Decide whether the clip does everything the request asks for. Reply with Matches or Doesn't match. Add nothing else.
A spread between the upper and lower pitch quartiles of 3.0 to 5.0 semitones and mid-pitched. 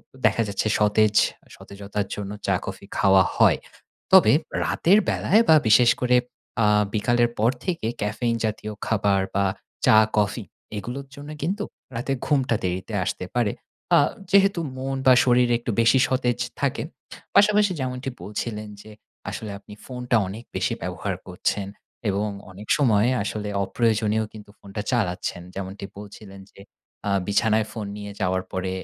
Doesn't match